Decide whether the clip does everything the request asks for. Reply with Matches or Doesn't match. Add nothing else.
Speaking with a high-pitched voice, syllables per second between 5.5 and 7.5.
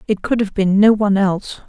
Matches